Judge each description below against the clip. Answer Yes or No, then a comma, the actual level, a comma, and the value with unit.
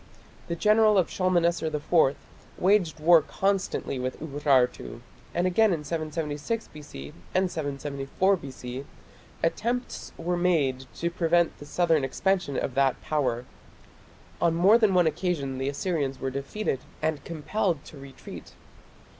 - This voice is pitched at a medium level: Yes, medium, 160 Hz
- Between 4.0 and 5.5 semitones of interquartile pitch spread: Yes, average, 4.7 semitones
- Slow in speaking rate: Yes, slow, 130 wpm